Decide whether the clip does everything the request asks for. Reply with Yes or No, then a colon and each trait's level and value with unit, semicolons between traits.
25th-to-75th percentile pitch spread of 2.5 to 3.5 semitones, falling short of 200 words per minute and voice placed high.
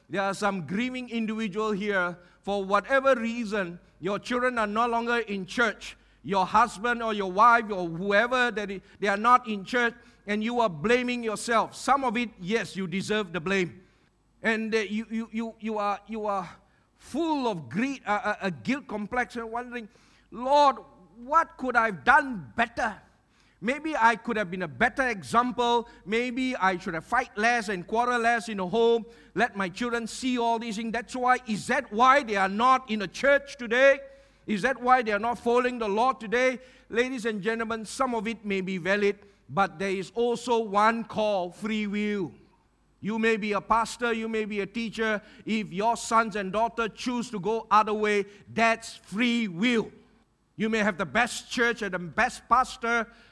Yes: average, 2.9 semitones; average, 185 wpm; high, 225 Hz